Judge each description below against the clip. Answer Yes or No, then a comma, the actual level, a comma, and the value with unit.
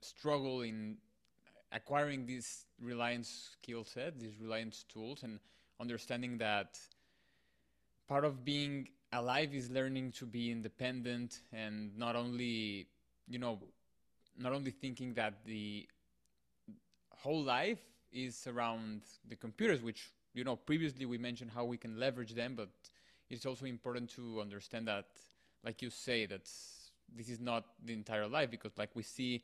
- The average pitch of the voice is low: Yes, low, 120 Hz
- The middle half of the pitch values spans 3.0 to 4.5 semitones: No, narrow, 2.6 semitones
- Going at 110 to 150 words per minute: Yes, average, 145 wpm